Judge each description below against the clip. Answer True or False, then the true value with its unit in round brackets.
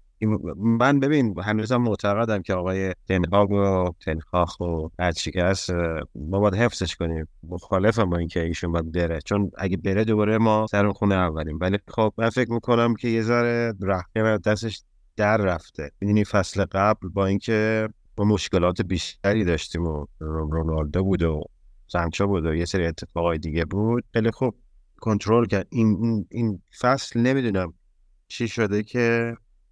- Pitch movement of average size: True (4.4 semitones)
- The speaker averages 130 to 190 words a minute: True (150 wpm)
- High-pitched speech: False (100 Hz)